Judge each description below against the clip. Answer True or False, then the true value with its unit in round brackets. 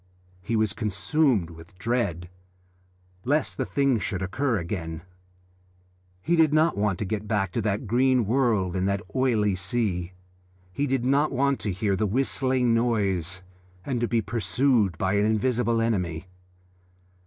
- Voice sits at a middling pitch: False (110 Hz)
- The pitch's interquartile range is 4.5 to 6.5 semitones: True (5.0 semitones)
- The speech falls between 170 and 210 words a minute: False (150 wpm)